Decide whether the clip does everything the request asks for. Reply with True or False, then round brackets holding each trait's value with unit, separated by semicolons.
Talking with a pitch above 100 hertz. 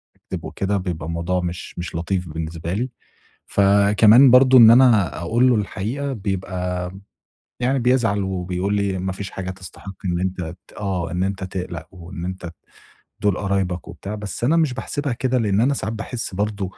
False (95 Hz)